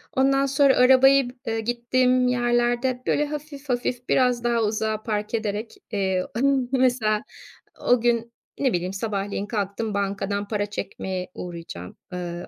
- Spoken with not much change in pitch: No, average, 3.8 semitones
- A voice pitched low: No, high, 235 Hz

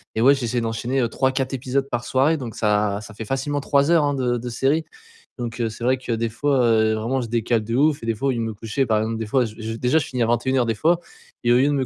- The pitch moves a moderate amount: Yes, average, 3.0 semitones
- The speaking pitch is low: Yes, low, 120 Hz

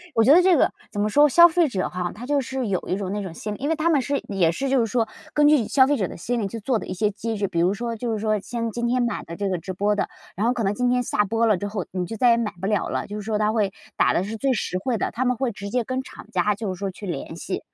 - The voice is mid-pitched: No, high, 220 Hz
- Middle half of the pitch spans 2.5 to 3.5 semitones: No, average, 3.9 semitones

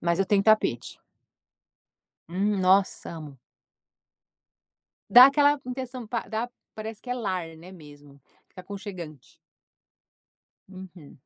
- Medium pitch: No, high, 195 Hz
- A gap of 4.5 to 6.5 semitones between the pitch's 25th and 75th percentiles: Yes, average, 4.8 semitones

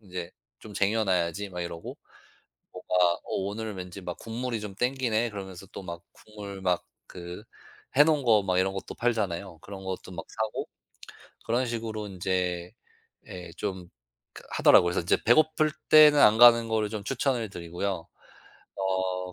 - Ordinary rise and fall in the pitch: Yes, average, 3.6 semitones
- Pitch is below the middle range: Yes, low, 100 Hz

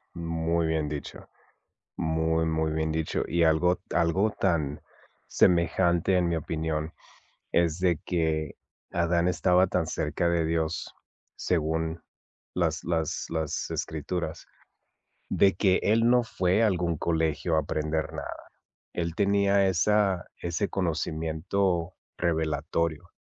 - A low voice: Yes, very low, 85 Hz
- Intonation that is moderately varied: No, narrow, 2.2 semitones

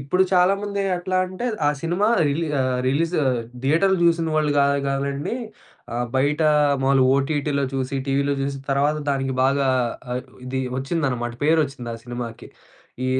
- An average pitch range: Yes, average, 3.8 semitones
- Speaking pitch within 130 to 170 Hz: Yes, medium, 140 Hz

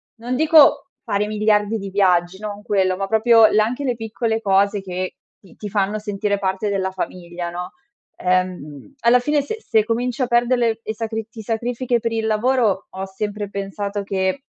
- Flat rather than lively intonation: No, average, 3.1 semitones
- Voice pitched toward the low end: No, high, 210 Hz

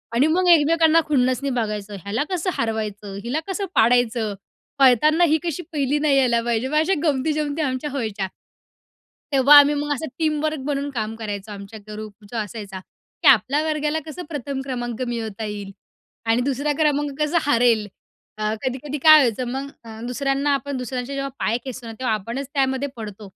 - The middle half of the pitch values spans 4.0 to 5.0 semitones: Yes, average, 4.7 semitones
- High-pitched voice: Yes, very high, 260 Hz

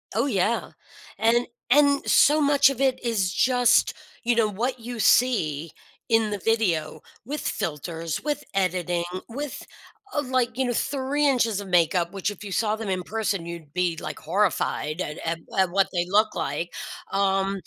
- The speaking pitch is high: Yes, high, 210 Hz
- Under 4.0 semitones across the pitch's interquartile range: No, wide, 5.6 semitones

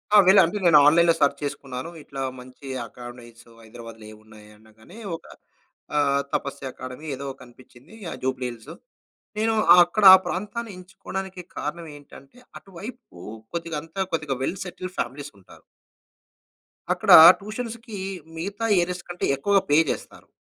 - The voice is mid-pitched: Yes, medium, 150 Hz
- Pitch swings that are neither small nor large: No, wide, 7.0 semitones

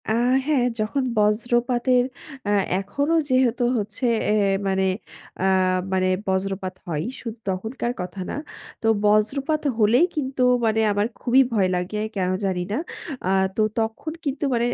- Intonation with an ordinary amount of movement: Yes, average, 4.6 semitones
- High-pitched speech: Yes, high, 220 Hz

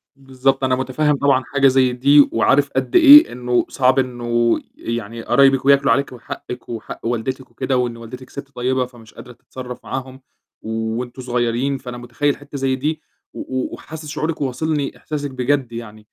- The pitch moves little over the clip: Yes, narrow, 2.2 semitones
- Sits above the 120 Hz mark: Yes, low, 130 Hz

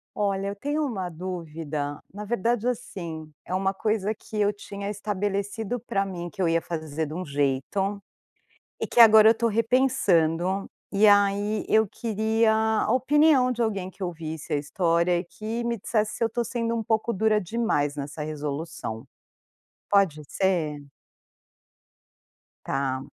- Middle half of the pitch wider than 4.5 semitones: Yes, average, 4.9 semitones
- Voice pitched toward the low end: No, high, 200 Hz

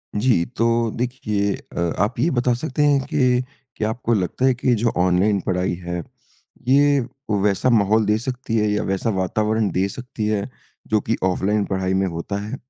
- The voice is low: Yes, low, 110 Hz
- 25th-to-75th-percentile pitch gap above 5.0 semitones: No, average, 4.1 semitones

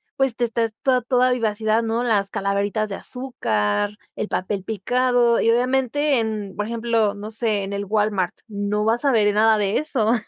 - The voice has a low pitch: No, high, 220 Hz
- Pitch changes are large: No, average, 2.8 semitones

